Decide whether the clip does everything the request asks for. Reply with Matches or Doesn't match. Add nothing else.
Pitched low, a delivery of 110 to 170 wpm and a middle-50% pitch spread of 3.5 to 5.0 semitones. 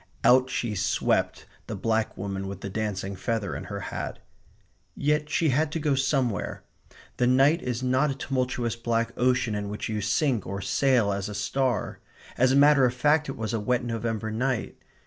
Doesn't match